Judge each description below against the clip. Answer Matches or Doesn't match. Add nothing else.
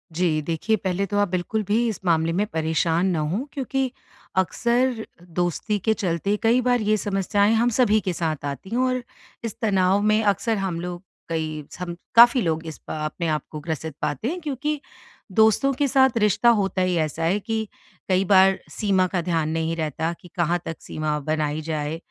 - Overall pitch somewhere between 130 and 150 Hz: Doesn't match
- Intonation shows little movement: Doesn't match